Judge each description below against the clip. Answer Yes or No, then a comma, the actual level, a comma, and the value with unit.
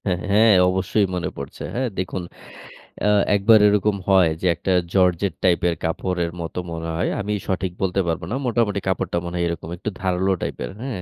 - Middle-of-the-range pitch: No, very low, 95 Hz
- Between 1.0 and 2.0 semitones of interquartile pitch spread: No, narrow, 2.5 semitones